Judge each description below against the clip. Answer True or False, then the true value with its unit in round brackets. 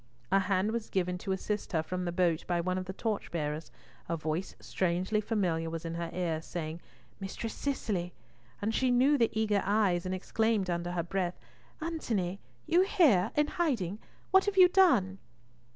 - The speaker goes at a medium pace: True (175 wpm)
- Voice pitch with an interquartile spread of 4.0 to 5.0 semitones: True (4.5 semitones)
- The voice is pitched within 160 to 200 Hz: True (190 Hz)